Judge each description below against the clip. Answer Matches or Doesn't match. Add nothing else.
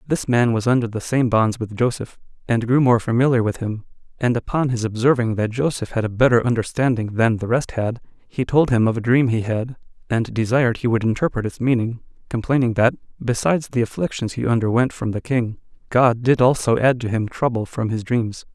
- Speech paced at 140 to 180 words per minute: Doesn't match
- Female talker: Doesn't match